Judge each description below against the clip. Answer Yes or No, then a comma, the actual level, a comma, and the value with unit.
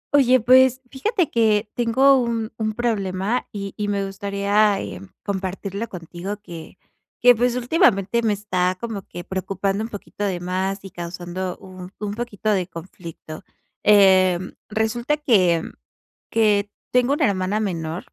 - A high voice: Yes, high, 205 Hz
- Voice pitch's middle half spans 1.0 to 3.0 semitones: No, average, 3.6 semitones